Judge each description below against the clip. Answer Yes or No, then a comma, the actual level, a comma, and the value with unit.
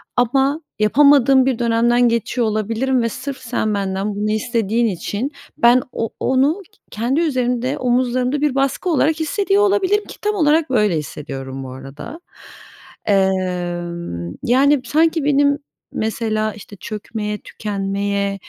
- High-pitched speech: Yes, high, 235 Hz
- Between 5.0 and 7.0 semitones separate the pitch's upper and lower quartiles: Yes, wide, 5.4 semitones